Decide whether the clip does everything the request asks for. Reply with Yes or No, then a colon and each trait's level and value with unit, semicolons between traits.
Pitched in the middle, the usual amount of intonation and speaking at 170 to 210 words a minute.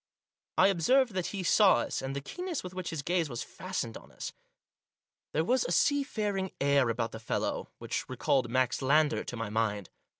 No: medium, 155 Hz; wide, 7.7 semitones; average, 190 wpm